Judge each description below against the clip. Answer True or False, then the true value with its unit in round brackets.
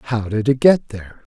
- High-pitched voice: False (115 Hz)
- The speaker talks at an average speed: False (220 wpm)